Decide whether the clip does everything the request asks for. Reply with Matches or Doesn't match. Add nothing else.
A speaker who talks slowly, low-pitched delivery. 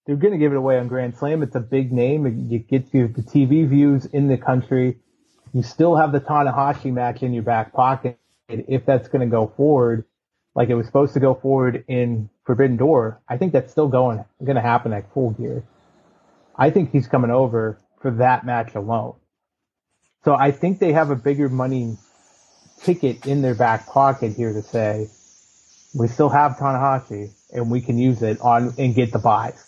Doesn't match